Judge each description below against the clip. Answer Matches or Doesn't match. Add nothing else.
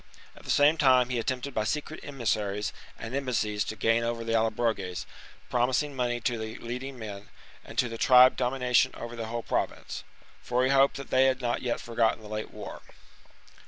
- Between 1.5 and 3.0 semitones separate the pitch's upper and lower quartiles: Matches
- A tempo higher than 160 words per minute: Matches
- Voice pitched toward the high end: Doesn't match